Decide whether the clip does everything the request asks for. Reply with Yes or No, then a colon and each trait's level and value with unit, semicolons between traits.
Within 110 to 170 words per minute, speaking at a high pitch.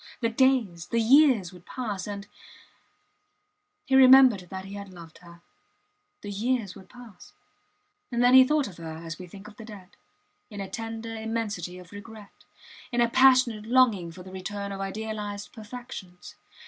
Yes: average, 165 wpm; high, 210 Hz